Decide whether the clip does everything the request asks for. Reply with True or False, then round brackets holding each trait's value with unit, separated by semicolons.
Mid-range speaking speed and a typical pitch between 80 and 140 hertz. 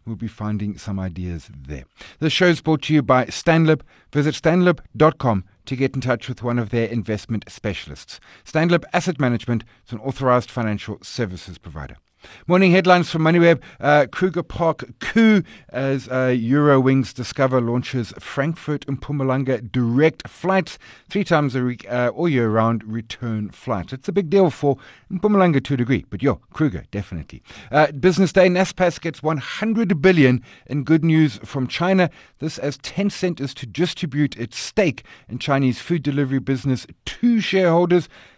True (160 wpm; 135 Hz)